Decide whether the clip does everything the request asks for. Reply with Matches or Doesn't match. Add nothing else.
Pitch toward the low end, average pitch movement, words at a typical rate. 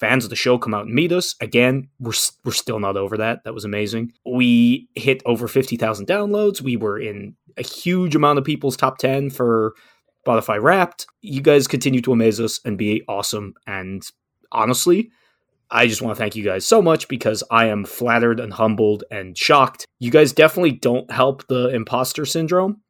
Matches